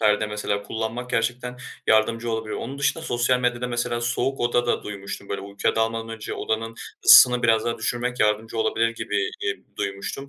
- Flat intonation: Yes, narrow, 2.1 semitones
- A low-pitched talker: Yes, low, 115 Hz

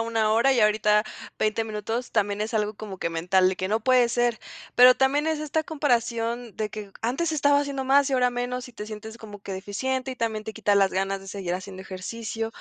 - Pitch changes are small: No, average, 3.5 semitones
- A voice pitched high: Yes, high, 225 Hz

